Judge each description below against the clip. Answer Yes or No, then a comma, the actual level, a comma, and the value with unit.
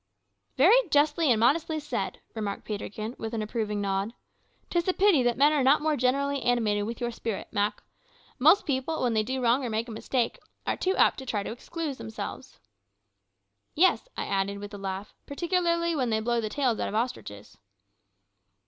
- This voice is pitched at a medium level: No, high, 245 Hz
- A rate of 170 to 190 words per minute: Yes, average, 185 wpm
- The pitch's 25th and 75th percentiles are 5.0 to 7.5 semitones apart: Yes, wide, 5.4 semitones